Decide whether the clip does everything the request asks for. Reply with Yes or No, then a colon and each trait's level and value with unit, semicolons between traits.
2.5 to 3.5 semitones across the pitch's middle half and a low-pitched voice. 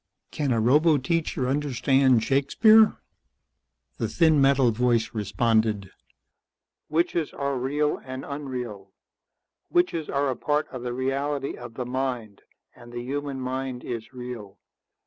Yes: average, 3.1 semitones; low, 130 Hz